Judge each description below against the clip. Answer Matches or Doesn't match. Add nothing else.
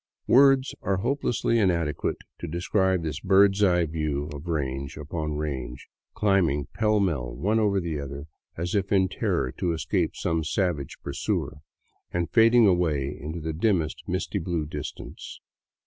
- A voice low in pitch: Matches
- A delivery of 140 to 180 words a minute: Matches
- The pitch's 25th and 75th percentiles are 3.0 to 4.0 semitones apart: Doesn't match